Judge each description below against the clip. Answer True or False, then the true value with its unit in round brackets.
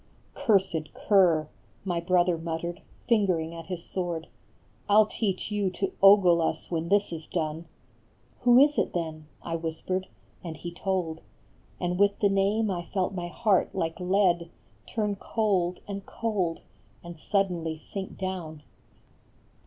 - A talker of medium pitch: True (180 Hz)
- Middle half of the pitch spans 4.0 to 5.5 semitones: False (3.1 semitones)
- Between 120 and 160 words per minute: True (155 wpm)